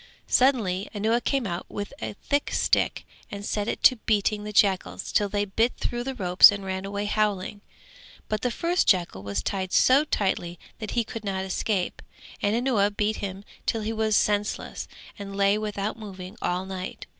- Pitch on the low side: No, high, 205 Hz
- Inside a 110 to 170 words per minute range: No, average, 180 wpm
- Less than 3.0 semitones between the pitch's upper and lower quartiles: Yes, narrow, 2.4 semitones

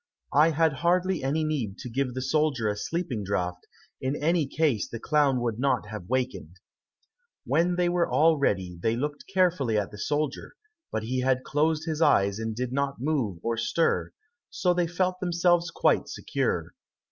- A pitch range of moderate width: No, wide, 6.2 semitones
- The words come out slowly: No, average, 175 wpm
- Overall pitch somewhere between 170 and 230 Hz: No, medium, 140 Hz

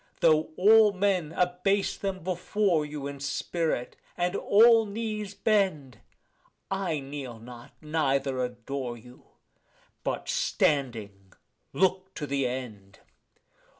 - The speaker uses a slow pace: Yes, slow, 110 wpm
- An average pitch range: No, wide, 6.9 semitones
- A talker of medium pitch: Yes, medium, 155 Hz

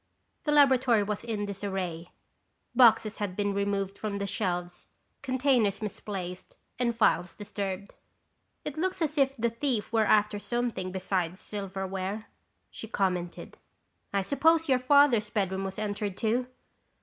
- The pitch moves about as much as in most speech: Yes, average, 3.9 semitones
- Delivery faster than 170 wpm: No, slow, 135 wpm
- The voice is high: Yes, high, 210 Hz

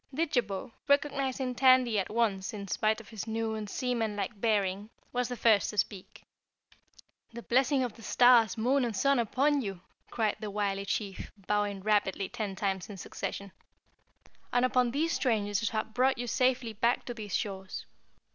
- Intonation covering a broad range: No, average, 3.6 semitones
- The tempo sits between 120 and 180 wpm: Yes, average, 170 wpm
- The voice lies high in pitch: Yes, high, 220 Hz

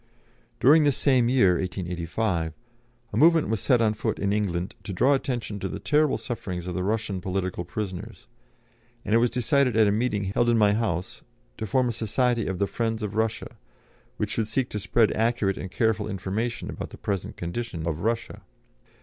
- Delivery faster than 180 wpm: Yes, average, 190 wpm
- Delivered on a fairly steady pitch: No, average, 4.0 semitones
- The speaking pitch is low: Yes, low, 110 Hz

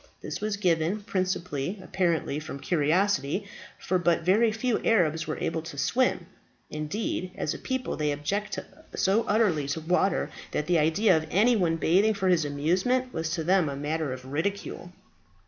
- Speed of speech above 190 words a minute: No, average, 165 wpm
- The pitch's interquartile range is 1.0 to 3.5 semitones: No, average, 4.7 semitones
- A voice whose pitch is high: No, medium, 175 Hz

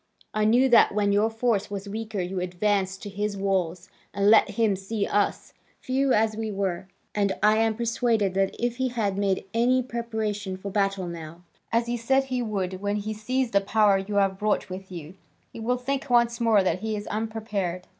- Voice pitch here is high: Yes, high, 210 Hz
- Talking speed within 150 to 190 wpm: No, average, 200 wpm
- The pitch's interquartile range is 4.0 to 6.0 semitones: No, average, 2.9 semitones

